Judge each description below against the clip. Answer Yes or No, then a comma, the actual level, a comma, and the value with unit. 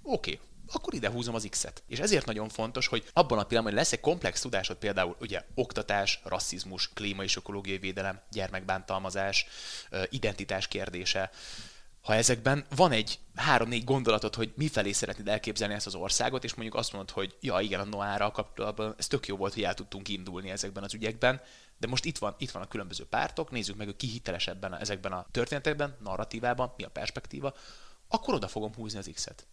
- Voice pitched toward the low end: Yes, low, 105 Hz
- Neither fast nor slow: No, fast, 185 wpm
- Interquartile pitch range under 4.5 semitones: Yes, average, 3.0 semitones